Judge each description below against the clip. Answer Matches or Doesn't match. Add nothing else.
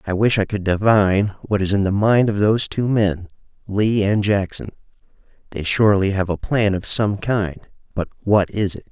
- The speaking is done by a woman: Doesn't match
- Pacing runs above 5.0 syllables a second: Doesn't match